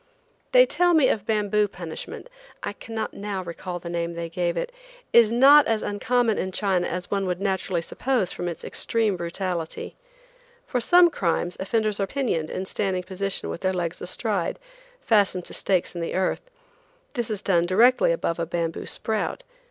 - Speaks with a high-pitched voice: Yes, high, 195 Hz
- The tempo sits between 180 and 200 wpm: No, average, 170 wpm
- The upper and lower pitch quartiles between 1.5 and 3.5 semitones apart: No, average, 4.3 semitones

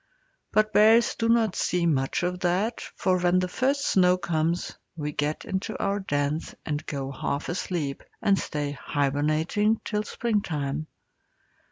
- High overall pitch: No, medium, 175 Hz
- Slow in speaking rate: No, average, 145 wpm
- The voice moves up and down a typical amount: No, wide, 5.8 semitones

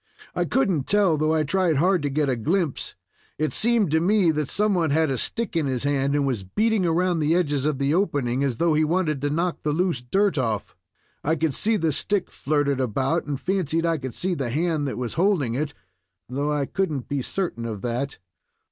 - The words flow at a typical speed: No, fast, 220 wpm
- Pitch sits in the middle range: Yes, medium, 155 Hz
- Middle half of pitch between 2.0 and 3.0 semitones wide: No, average, 4.5 semitones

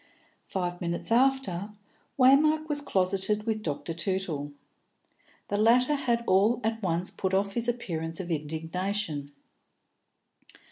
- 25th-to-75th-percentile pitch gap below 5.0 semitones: No, wide, 5.5 semitones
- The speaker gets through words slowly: Yes, slow, 120 wpm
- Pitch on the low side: No, high, 195 Hz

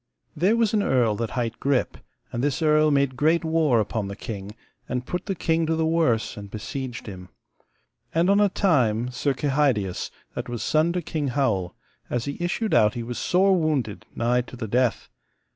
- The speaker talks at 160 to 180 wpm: No, average, 195 wpm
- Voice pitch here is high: No, low, 135 Hz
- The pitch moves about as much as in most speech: No, wide, 5.8 semitones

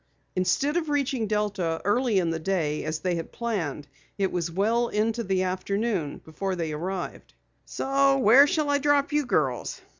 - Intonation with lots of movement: Yes, wide, 7.1 semitones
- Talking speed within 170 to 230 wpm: No, average, 160 wpm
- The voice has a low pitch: No, high, 200 Hz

